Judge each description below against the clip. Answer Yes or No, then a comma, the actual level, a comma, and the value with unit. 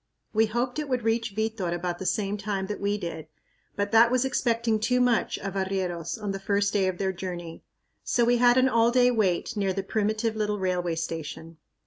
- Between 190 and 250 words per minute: Yes, fast, 205 wpm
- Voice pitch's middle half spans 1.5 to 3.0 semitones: No, average, 3.5 semitones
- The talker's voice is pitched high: Yes, high, 205 Hz